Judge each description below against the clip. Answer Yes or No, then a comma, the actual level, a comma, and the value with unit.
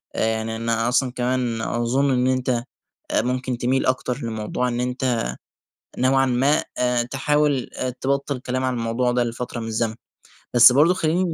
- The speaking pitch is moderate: No, low, 125 Hz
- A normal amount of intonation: No, narrow, 1.7 semitones